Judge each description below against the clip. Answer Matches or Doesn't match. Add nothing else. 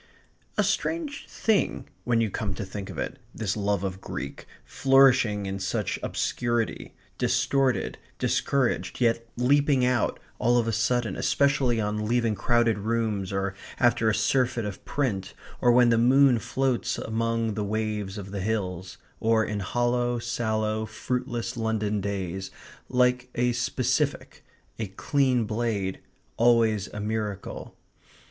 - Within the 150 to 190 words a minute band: Doesn't match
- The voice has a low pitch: Matches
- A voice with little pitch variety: Doesn't match